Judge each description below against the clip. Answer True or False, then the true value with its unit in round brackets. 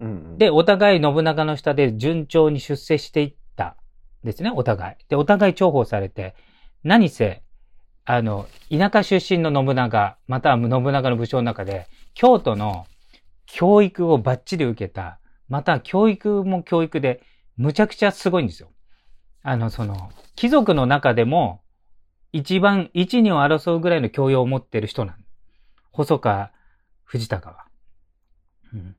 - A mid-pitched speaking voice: False (130 Hz)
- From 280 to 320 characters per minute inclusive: False (265 characters per minute)